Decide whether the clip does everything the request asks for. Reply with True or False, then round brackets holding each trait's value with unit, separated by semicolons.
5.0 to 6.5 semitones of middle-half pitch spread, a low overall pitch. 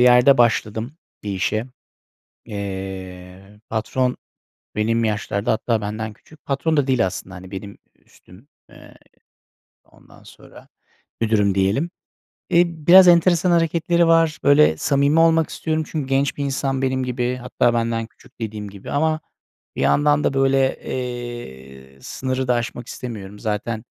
True (5.3 semitones; 120 Hz)